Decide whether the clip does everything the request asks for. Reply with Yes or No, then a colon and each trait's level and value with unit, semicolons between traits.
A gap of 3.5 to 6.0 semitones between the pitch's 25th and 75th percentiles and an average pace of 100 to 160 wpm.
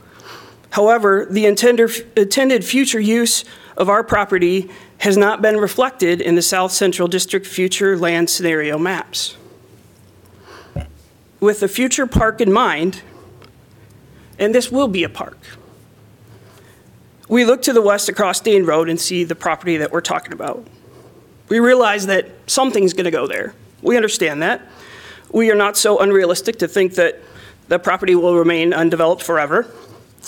Yes: average, 4.4 semitones; average, 145 wpm